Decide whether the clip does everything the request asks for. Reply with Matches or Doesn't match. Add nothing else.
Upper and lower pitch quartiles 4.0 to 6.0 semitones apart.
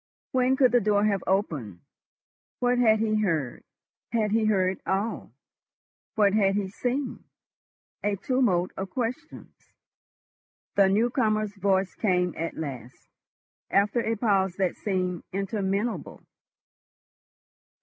Doesn't match